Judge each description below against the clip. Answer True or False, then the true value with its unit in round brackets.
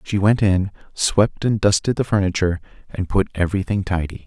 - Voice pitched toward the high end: False (100 Hz)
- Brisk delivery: False (170 wpm)